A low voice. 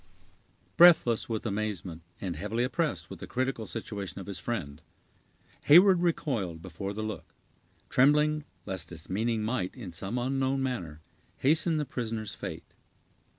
Yes: low, 115 Hz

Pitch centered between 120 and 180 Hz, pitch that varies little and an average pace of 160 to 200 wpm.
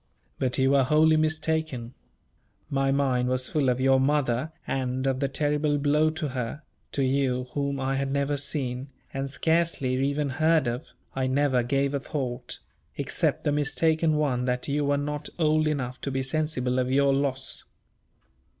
Yes: medium, 140 Hz; narrow, 2.3 semitones; average, 170 wpm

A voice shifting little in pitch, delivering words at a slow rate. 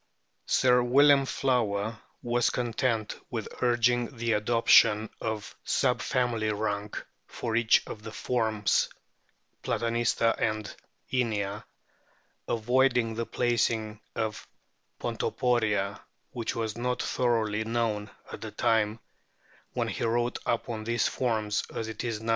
Yes: narrow, 1.9 semitones; slow, 125 wpm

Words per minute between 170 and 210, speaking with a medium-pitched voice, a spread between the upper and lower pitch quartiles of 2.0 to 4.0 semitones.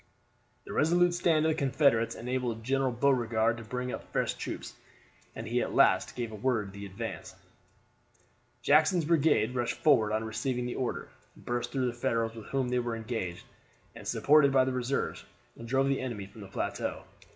No: average, 175 wpm; low, 125 Hz; average, 3.2 semitones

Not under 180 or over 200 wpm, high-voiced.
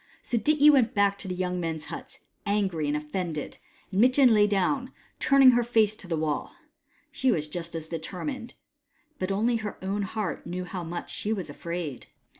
Yes: average, 185 wpm; high, 195 Hz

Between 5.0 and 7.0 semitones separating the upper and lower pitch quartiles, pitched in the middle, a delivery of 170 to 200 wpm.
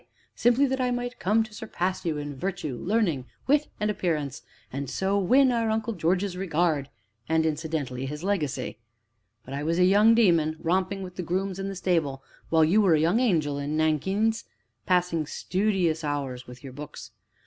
Yes: average, 5.3 semitones; medium, 175 Hz; average, 180 wpm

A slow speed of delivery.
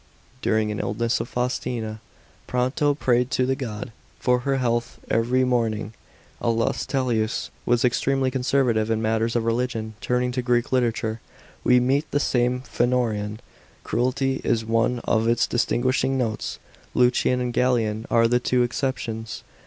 No: average, 155 wpm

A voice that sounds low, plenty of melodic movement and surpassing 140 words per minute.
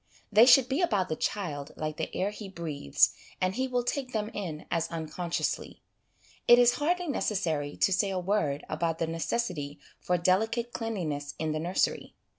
No: medium, 185 Hz; wide, 6.5 semitones; average, 175 wpm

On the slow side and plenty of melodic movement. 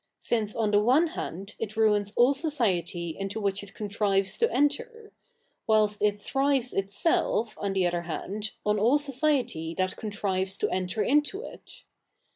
No: average, 155 wpm; wide, 5.7 semitones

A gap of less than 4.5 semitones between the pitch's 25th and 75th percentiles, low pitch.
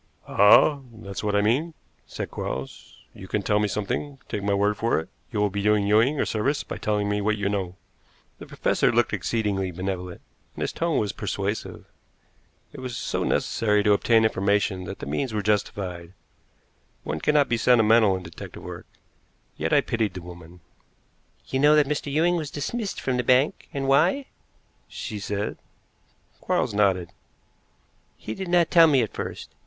No: average, 5.2 semitones; low, 105 Hz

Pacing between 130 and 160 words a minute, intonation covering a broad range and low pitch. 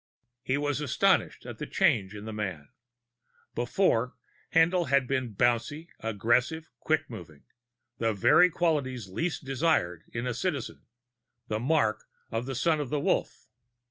Yes: average, 140 wpm; wide, 5.7 semitones; low, 130 Hz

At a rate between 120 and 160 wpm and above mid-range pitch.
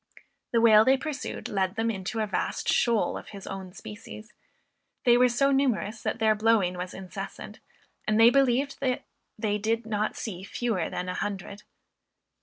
No: average, 170 wpm; high, 220 Hz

